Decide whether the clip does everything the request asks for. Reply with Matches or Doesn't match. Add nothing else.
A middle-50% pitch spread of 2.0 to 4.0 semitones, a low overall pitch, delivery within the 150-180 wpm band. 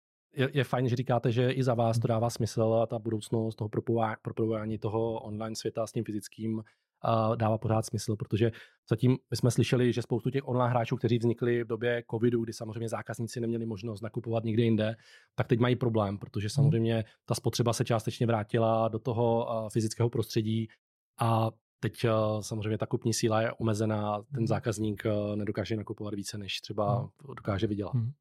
Doesn't match